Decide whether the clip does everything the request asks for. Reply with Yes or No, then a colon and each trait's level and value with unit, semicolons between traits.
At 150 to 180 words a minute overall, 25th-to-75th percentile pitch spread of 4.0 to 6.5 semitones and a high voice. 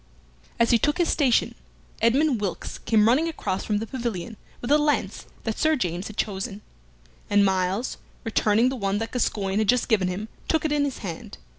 No: average, 190 wpm; average, 4.6 semitones; high, 225 Hz